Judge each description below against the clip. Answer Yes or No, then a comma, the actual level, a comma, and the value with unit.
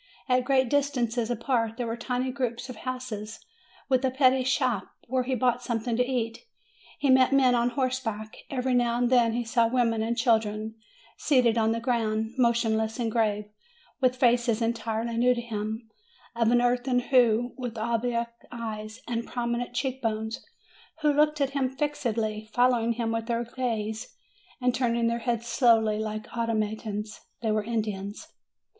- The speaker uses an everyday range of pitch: No, narrow, 2.1 semitones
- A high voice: Yes, high, 235 Hz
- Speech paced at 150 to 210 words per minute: Yes, average, 165 wpm